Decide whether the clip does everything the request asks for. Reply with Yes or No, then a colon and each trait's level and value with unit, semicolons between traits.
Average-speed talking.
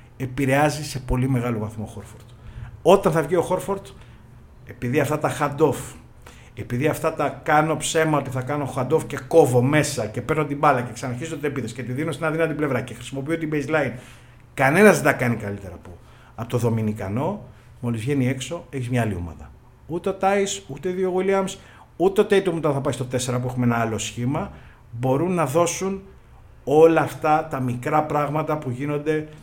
No: fast, 190 wpm